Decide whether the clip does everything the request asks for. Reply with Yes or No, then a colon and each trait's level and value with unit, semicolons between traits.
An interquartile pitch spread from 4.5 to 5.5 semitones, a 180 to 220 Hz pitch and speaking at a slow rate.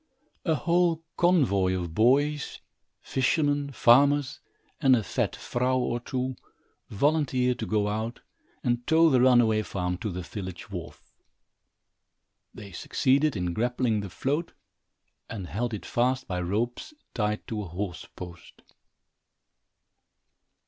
No: average, 5.2 semitones; low, 120 Hz; slow, 125 wpm